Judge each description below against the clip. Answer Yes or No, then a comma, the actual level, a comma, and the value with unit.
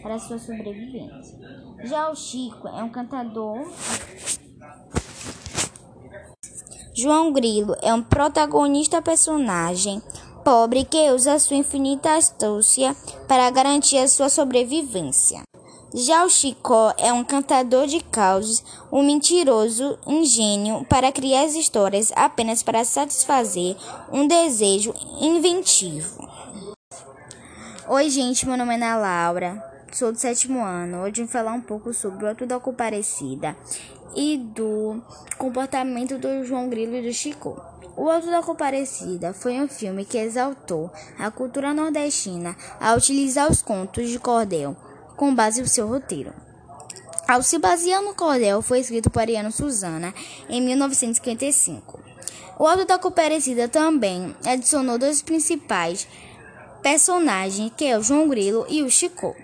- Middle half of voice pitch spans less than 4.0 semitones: No, average, 4.8 semitones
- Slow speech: No, average, 130 wpm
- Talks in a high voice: Yes, very high, 250 Hz